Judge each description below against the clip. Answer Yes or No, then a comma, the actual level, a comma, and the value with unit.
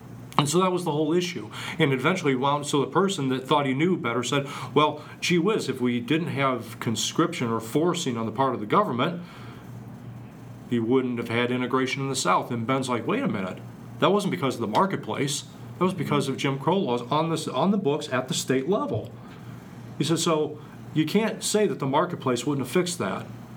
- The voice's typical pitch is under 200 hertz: Yes, medium, 140 Hz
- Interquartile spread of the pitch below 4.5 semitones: Yes, average, 3.9 semitones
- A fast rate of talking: Yes, fast, 215 wpm